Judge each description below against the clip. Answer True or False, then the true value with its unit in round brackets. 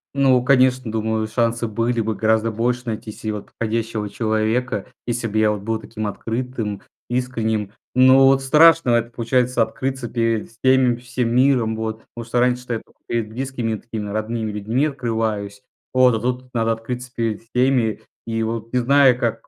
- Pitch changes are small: True (2.2 semitones)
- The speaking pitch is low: True (115 Hz)